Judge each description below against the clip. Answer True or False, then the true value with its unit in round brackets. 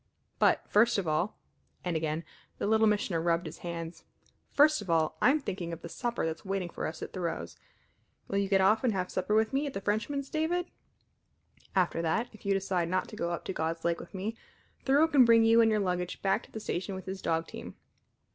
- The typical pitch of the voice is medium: False (195 Hz)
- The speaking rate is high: True (220 wpm)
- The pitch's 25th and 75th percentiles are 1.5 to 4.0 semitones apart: False (4.6 semitones)